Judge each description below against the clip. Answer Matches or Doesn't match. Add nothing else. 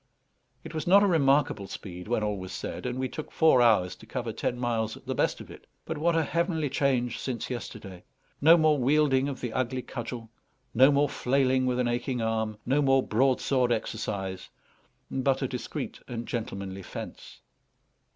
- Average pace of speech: Matches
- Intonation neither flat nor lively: Matches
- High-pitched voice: Doesn't match